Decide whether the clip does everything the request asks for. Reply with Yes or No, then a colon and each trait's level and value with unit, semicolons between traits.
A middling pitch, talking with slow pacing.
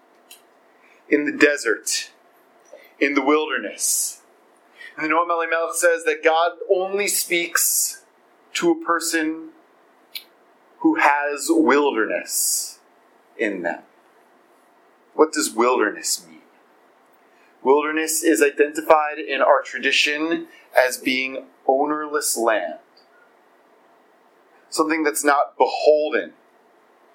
Yes: medium, 170 Hz; slow, 90 wpm